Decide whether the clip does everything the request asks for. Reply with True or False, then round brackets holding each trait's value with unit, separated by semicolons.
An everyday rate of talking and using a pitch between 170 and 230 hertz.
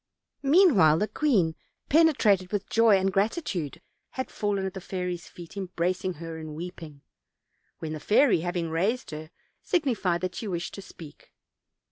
True (150 wpm; 185 Hz)